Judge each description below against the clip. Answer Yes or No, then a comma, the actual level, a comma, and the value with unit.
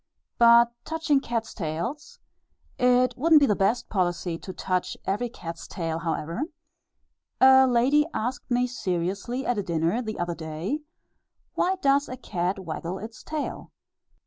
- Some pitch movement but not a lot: No, wide, 6.4 semitones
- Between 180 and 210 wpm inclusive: No, average, 140 wpm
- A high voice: Yes, high, 225 Hz